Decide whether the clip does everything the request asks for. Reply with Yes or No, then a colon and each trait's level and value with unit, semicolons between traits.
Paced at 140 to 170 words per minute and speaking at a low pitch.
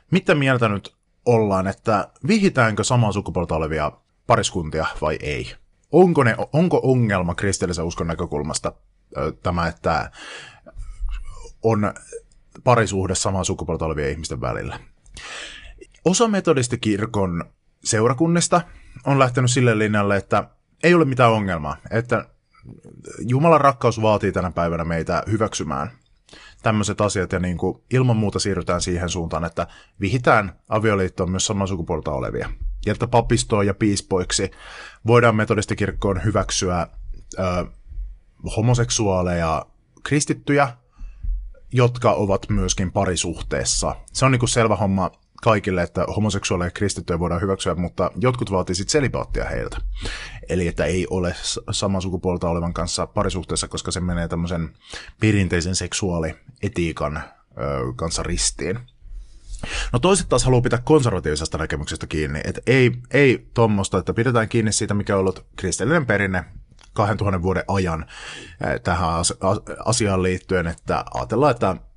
No: average, 120 wpm; low, 100 Hz